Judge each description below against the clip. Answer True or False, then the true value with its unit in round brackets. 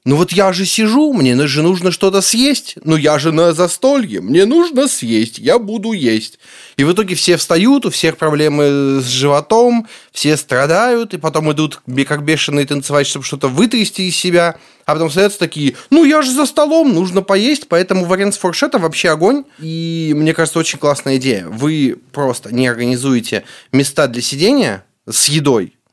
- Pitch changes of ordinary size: False (6.0 semitones)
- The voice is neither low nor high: True (165 Hz)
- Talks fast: True (175 wpm)